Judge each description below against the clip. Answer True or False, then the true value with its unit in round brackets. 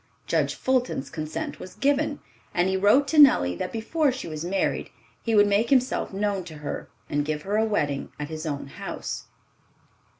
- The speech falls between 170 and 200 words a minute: True (185 wpm)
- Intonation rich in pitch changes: True (8.2 semitones)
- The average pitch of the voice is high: True (195 Hz)